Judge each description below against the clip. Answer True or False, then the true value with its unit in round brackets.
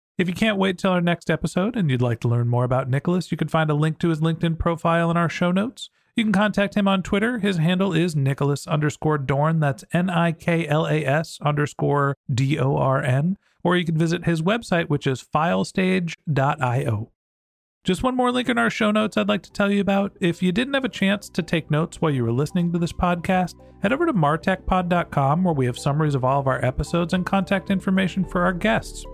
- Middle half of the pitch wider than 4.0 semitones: True (4.7 semitones)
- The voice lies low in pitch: False (170 Hz)